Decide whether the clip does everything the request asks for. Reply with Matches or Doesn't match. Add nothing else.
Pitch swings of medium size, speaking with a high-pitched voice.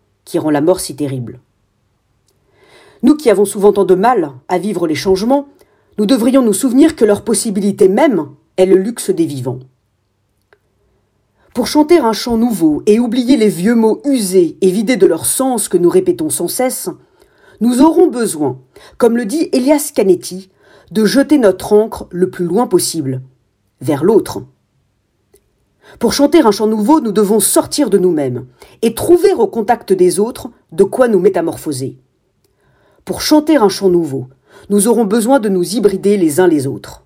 Doesn't match